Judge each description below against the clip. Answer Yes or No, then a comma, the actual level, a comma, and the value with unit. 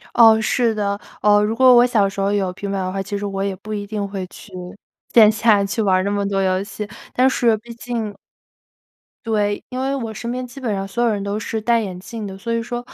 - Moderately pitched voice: No, high, 210 Hz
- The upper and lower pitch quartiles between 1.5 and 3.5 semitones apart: Yes, average, 2.8 semitones